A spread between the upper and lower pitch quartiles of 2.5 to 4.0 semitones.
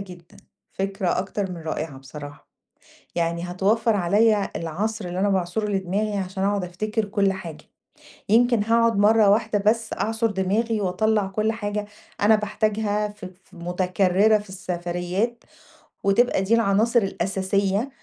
Yes: average, 2.9 semitones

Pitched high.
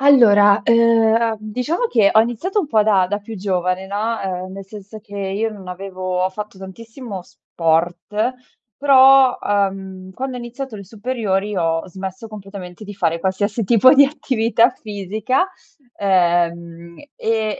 Yes: high, 205 Hz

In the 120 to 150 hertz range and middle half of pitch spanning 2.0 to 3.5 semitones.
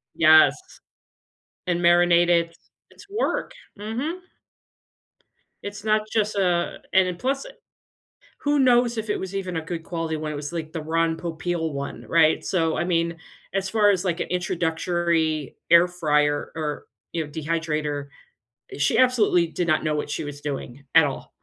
No: medium, 170 Hz; average, 3.2 semitones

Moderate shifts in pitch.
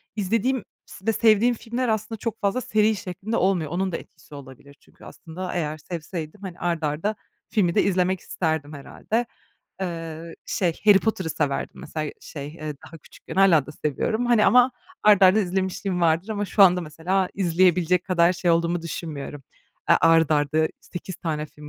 Yes: average, 4.2 semitones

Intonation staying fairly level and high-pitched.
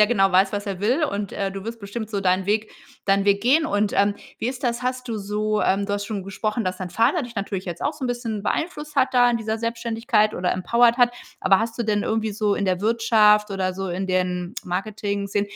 No: average, 3.0 semitones; high, 210 Hz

